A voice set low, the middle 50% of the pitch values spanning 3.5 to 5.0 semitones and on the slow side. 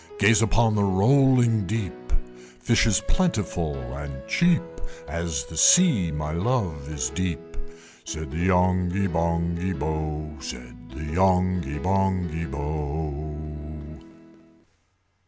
Yes: very low, 85 Hz; average, 4.2 semitones; slow, 105 wpm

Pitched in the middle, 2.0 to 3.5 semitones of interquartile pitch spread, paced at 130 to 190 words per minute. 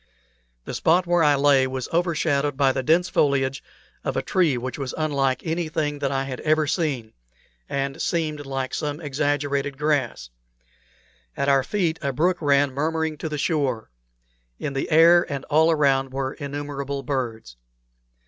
Yes: medium, 145 Hz; narrow, 2.6 semitones; average, 160 wpm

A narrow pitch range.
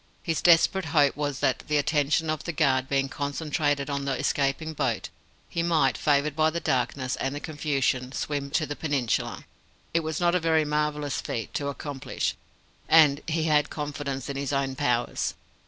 Yes: narrow, 2.2 semitones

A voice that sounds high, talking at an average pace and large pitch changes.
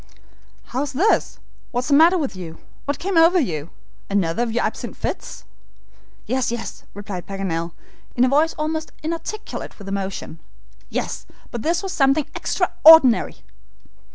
Yes: very high, 255 Hz; average, 145 wpm; wide, 8.3 semitones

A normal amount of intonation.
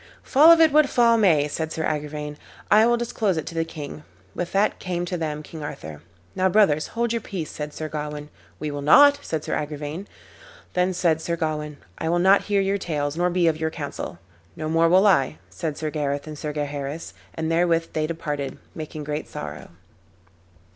Yes: average, 3.7 semitones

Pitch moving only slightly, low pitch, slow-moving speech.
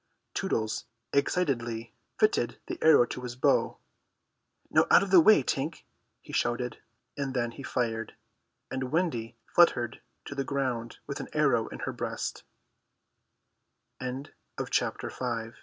No: average, 3.2 semitones; low, 125 Hz; slow, 110 wpm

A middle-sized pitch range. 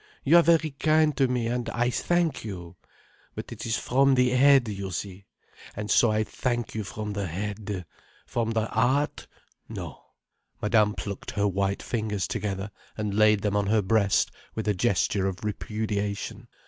Yes: average, 3.4 semitones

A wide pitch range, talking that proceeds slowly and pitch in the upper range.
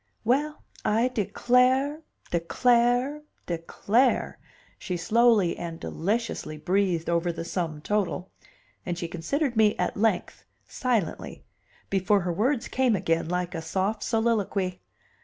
Yes: wide, 5.7 semitones; slow, 120 wpm; high, 200 Hz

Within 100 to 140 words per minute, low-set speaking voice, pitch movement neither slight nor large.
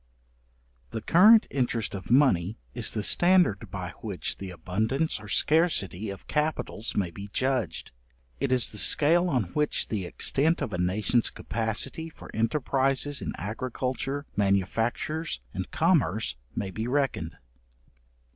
No: slow, 135 wpm; low, 115 Hz; wide, 6.5 semitones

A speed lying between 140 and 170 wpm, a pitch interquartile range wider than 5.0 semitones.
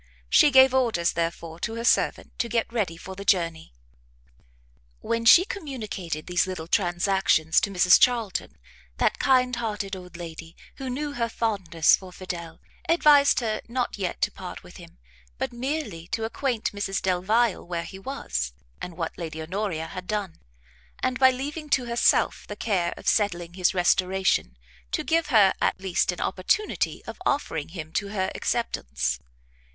Yes: average, 160 wpm; wide, 5.5 semitones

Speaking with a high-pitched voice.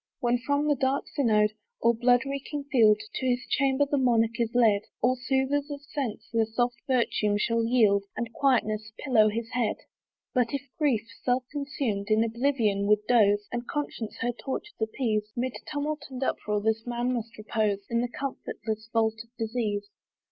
Yes: high, 235 Hz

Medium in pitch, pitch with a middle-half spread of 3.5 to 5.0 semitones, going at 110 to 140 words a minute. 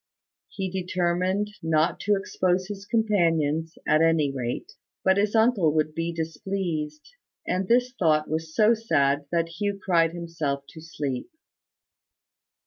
Yes: medium, 170 Hz; average, 3.9 semitones; slow, 135 wpm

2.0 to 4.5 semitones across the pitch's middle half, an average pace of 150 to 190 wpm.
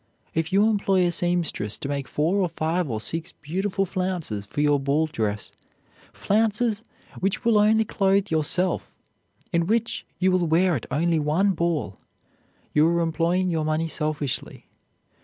Yes: average, 4.0 semitones; average, 155 wpm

